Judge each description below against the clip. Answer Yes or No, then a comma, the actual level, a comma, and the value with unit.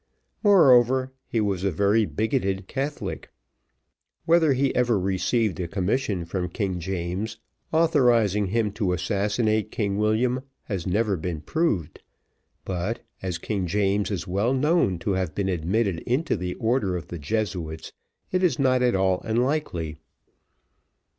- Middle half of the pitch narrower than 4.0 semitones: No, average, 5.2 semitones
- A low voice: Yes, low, 105 Hz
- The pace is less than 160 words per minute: Yes, average, 140 wpm